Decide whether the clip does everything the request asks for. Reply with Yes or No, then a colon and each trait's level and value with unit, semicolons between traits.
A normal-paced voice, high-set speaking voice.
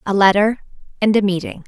Yes: average, 180 wpm; high, 200 Hz